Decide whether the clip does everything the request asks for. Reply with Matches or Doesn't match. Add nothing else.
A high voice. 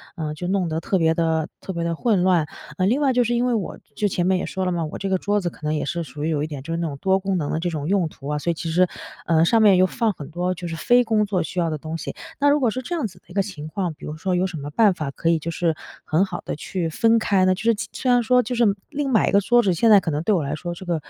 Doesn't match